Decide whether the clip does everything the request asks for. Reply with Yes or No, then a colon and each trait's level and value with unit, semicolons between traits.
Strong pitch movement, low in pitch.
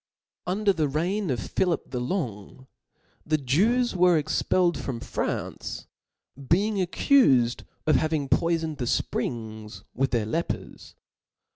No: wide, 6.2 semitones; medium, 155 Hz